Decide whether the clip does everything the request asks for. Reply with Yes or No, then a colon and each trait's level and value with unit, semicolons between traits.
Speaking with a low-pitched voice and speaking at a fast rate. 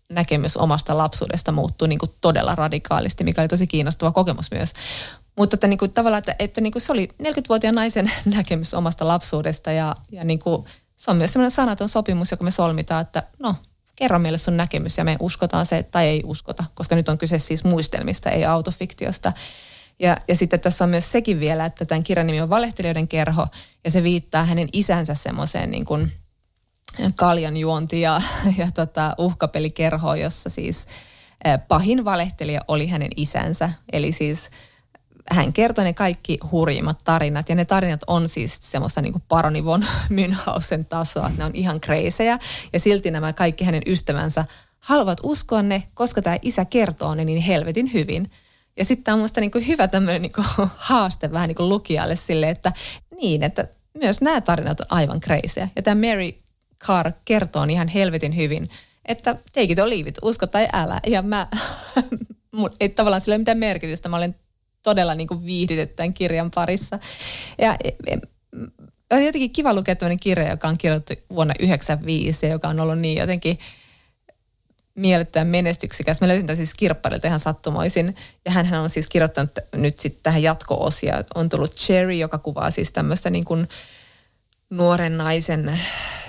No: medium, 170 Hz; fast, 170 wpm